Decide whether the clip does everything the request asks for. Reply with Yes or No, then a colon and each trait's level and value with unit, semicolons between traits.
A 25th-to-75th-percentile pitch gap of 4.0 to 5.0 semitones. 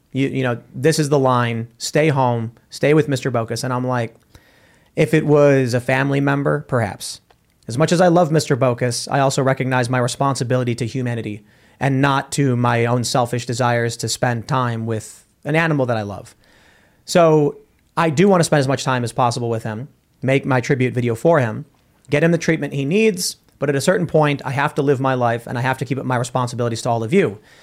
No: average, 3.2 semitones